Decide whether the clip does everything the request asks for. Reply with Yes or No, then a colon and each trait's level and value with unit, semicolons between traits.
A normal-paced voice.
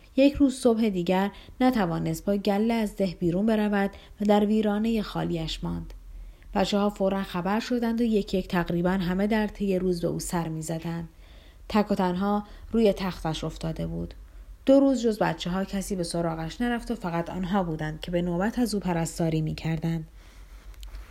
No: fast, 175 wpm